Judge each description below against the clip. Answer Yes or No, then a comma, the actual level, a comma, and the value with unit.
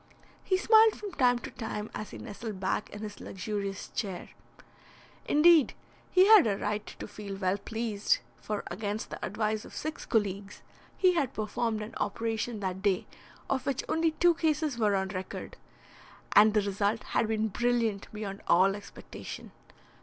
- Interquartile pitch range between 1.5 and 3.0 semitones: No, average, 3.6 semitones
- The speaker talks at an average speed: Yes, average, 160 wpm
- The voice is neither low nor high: No, high, 215 Hz